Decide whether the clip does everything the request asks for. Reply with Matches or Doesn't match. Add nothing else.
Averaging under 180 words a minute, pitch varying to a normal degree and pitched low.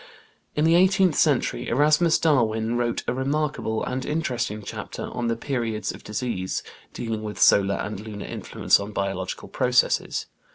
Doesn't match